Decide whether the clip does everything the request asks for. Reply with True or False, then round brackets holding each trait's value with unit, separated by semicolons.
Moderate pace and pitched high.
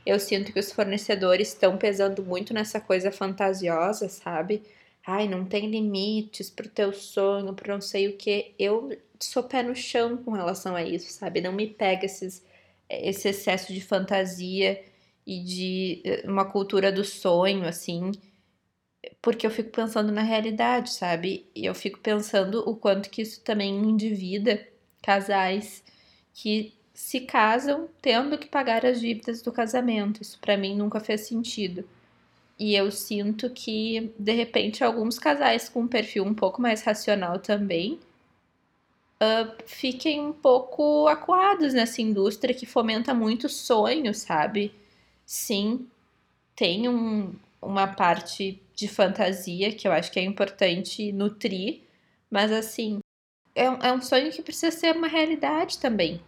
True (145 wpm; 210 Hz)